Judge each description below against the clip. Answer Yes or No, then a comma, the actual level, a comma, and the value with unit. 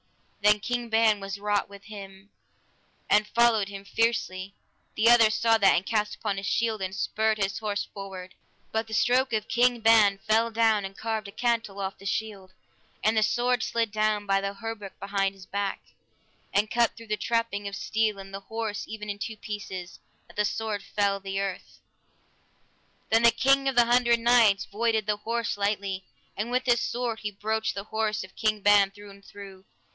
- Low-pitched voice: No, high, 210 Hz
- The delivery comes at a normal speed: Yes, average, 195 wpm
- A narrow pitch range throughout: Yes, narrow, 2.3 semitones